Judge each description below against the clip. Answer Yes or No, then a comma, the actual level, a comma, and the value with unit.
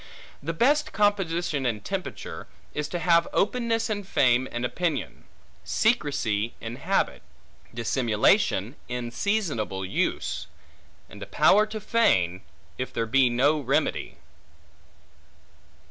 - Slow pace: Yes, slow, 115 wpm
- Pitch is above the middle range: No, medium, 145 Hz